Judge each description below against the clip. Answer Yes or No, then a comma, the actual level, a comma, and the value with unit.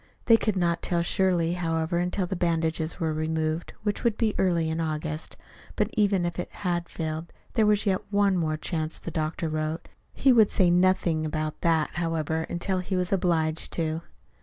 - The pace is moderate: Yes, average, 185 wpm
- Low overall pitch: No, medium, 170 Hz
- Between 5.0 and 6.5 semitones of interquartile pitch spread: No, average, 2.7 semitones